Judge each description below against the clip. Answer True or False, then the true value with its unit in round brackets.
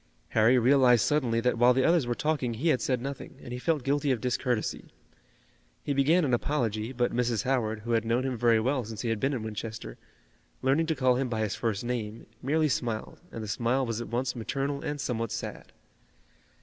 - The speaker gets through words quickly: True (210 wpm)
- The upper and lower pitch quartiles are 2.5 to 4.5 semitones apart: True (3.0 semitones)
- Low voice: True (125 Hz)